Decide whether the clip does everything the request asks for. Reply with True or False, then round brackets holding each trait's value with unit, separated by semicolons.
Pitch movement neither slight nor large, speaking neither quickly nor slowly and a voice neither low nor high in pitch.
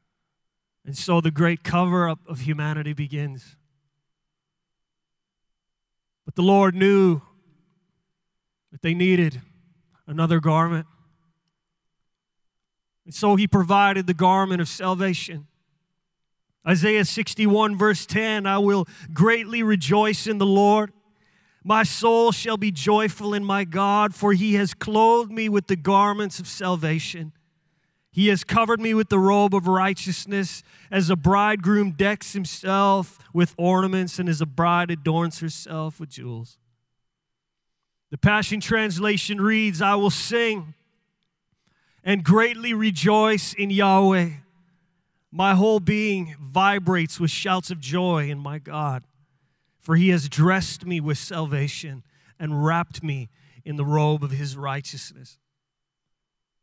False (4.1 semitones; 125 wpm; 180 Hz)